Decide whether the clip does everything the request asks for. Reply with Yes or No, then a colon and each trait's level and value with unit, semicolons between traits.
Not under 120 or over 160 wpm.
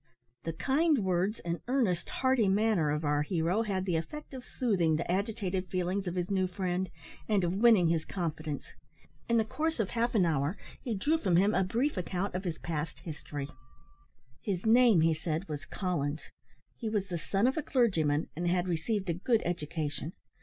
No: average, 190 wpm